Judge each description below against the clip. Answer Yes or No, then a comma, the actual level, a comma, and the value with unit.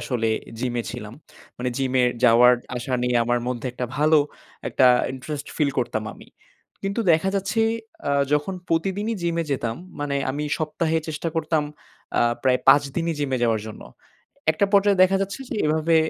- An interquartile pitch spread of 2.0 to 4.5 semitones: No, average, 5.1 semitones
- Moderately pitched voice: Yes, medium, 145 Hz